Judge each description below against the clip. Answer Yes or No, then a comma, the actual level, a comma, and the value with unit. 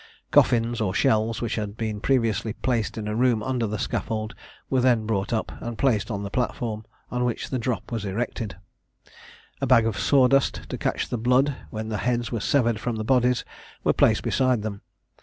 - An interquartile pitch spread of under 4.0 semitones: Yes, narrow, 2.4 semitones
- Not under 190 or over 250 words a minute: Yes, average, 195 wpm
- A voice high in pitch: No, low, 115 Hz